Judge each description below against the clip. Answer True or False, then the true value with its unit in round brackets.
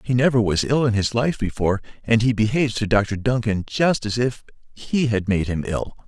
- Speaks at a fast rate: True (215 wpm)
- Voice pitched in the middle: False (115 Hz)